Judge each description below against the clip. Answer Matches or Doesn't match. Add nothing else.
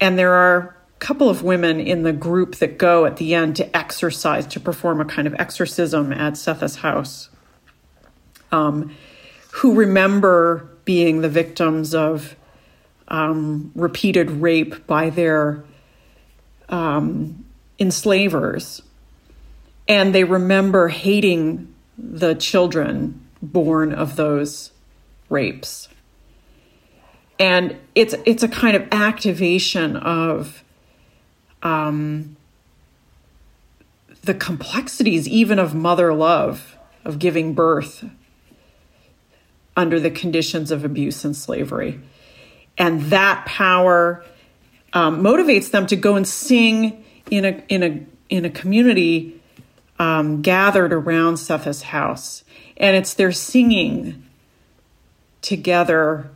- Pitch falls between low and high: Matches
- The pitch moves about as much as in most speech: Matches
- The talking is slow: Matches